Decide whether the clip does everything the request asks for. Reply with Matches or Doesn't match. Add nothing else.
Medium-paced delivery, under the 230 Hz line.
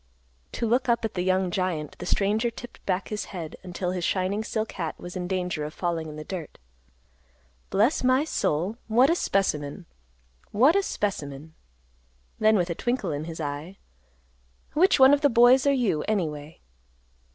Matches